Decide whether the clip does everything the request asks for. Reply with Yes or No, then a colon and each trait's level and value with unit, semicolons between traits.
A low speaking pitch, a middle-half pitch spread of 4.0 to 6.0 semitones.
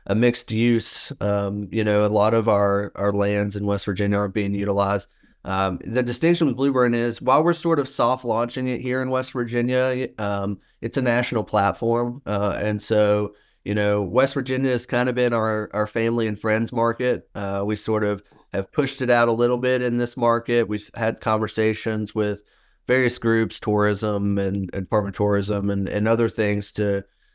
No: low, 110 Hz; average, 3.0 semitones